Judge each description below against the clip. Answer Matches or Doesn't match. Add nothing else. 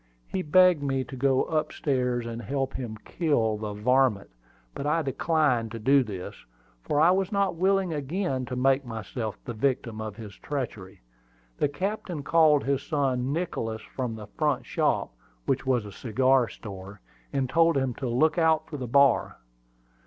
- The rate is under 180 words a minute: Matches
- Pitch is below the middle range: Matches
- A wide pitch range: Doesn't match